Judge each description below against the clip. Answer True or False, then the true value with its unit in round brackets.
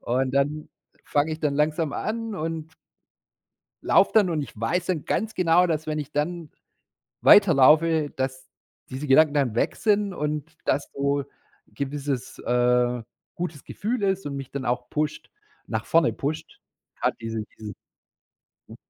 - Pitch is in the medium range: True (150 Hz)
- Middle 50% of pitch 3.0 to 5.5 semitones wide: True (3.5 semitones)